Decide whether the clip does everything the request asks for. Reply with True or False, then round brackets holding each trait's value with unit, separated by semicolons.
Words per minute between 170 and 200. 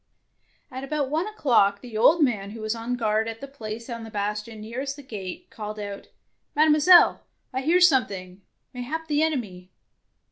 True (185 wpm)